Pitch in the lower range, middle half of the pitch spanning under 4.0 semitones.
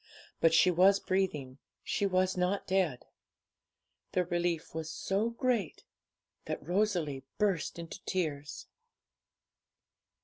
No: medium, 180 Hz; average, 3.2 semitones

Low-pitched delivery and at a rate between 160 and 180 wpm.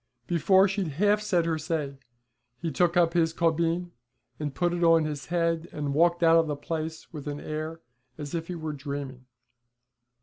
No: medium, 165 Hz; average, 175 wpm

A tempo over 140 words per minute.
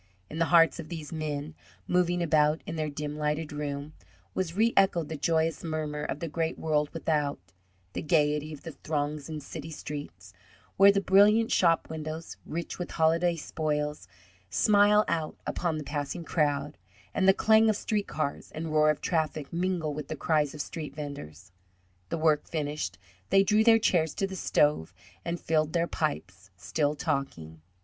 Yes: average, 170 wpm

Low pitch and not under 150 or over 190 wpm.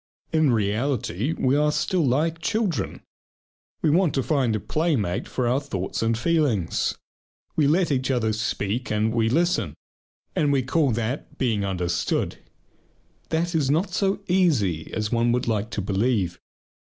Yes: low, 125 Hz; average, 155 wpm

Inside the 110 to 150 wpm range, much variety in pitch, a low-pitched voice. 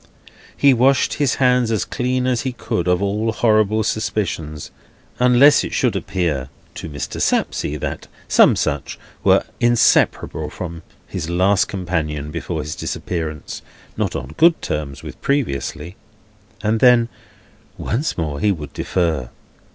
Yes: slow, 135 wpm; wide, 7.8 semitones; very low, 95 Hz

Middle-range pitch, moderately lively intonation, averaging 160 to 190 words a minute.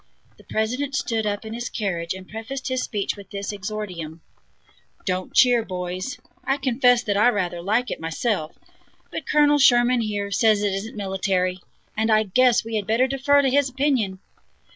No: high, 220 Hz; average, 4.4 semitones; average, 175 wpm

